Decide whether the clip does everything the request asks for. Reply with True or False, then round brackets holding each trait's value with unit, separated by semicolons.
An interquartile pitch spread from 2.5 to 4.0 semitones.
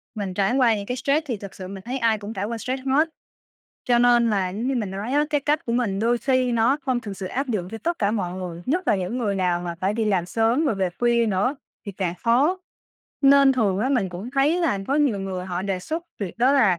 False (5.1 semitones)